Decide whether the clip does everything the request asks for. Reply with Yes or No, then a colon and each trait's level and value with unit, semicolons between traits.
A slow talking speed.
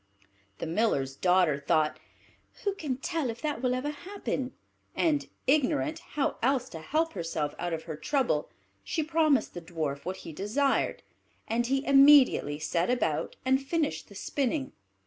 No: average, 155 wpm